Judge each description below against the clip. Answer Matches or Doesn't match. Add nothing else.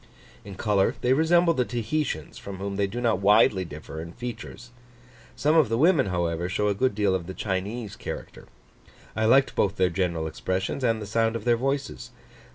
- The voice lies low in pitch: Matches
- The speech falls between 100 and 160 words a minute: Doesn't match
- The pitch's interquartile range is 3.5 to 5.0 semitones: Matches